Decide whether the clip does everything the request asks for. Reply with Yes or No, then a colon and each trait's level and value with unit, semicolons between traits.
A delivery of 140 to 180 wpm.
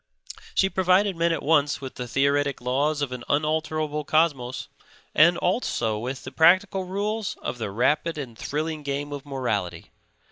Yes: average, 155 wpm